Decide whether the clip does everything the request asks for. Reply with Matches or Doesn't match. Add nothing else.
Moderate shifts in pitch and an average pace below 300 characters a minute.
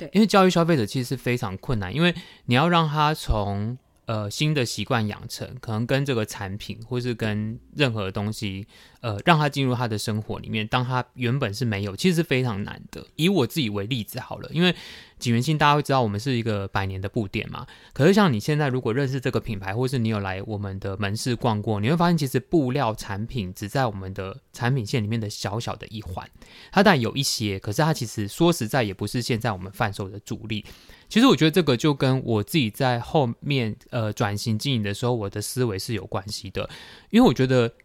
Doesn't match